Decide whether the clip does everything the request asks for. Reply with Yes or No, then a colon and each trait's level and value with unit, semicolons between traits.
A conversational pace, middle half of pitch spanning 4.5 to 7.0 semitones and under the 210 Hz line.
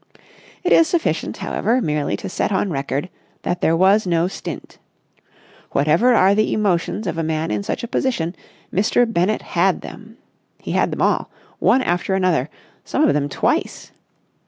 Yes: average, 165 wpm; average, 5.0 semitones; medium, 185 Hz